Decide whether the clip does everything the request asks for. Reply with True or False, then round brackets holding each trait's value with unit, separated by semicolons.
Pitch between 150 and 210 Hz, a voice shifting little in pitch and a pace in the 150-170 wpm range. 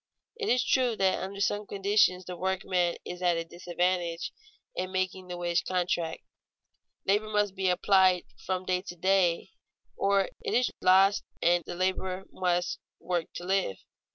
True (185 Hz; 1.7 semitones; 155 wpm)